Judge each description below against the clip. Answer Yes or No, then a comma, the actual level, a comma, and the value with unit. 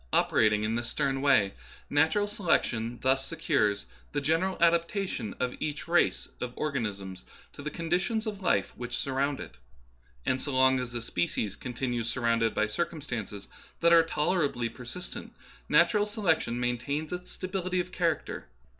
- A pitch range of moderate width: No, wide, 6.5 semitones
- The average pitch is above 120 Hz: Yes, medium, 140 Hz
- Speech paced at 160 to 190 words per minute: No, average, 150 wpm